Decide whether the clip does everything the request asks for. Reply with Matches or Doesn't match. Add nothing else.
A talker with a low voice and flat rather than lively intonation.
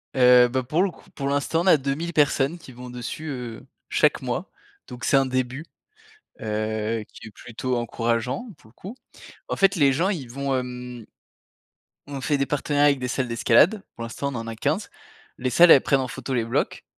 Doesn't match